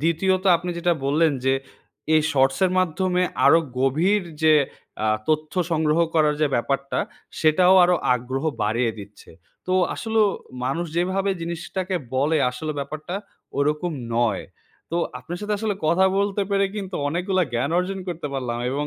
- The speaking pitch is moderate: Yes, medium, 160 Hz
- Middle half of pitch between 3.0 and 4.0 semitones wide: No, average, 4.9 semitones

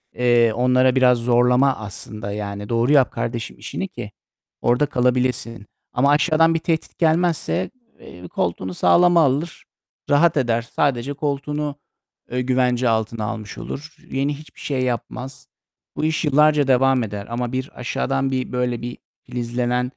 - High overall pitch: No, low, 125 Hz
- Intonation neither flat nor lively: Yes, average, 3.3 semitones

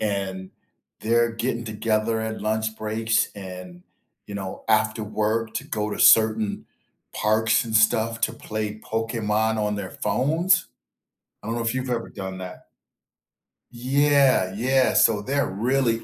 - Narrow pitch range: Yes, narrow, 1.8 semitones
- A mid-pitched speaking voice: No, low, 110 Hz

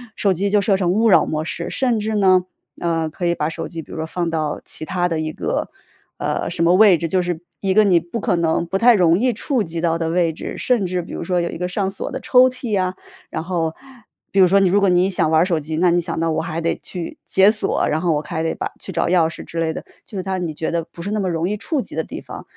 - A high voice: No, medium, 180 Hz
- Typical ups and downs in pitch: Yes, average, 3.1 semitones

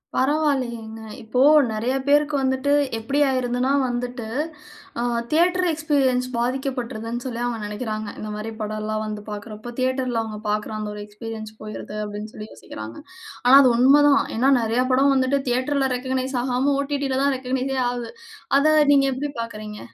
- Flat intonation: No, average, 3.7 semitones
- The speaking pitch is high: Yes, very high, 250 Hz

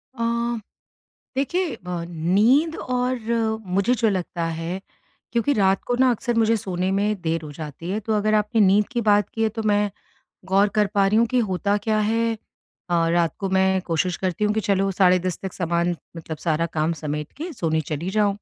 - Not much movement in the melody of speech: No, average, 4.0 semitones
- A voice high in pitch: Yes, high, 195 Hz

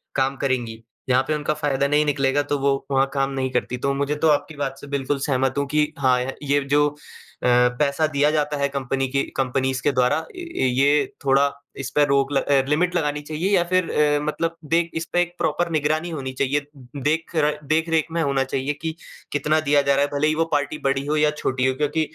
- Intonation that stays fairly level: Yes, narrow, 2.1 semitones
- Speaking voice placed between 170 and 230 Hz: No, medium, 145 Hz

